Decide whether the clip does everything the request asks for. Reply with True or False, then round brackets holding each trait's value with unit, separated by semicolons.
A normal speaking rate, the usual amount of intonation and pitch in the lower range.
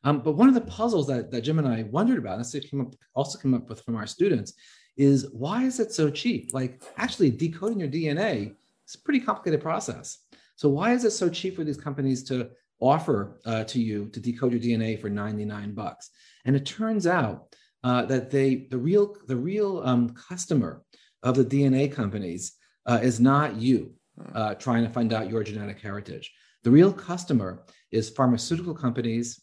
False (195 wpm; 5.9 semitones; 130 Hz)